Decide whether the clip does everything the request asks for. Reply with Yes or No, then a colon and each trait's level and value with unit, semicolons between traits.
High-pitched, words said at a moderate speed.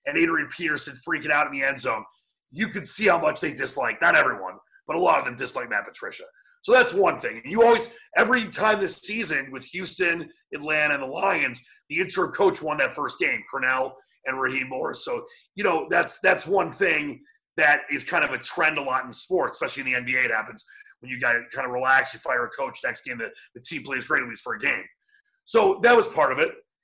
No: high, 215 Hz; fast, 235 wpm